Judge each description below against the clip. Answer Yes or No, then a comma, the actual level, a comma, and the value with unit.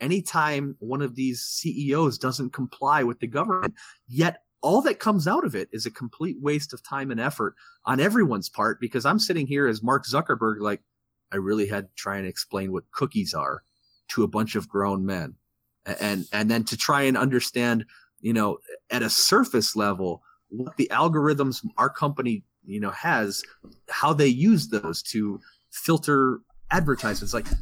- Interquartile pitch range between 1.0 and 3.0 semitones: No, average, 5.2 semitones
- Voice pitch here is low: Yes, low, 125 Hz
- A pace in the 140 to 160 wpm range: No, average, 175 wpm